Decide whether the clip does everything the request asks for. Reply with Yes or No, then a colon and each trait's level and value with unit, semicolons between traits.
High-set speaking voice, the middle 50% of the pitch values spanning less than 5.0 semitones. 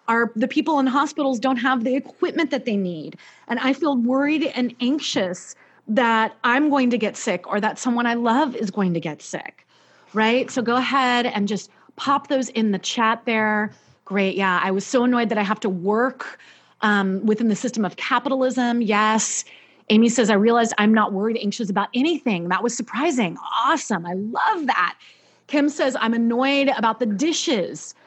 Yes: high, 235 Hz; average, 3.9 semitones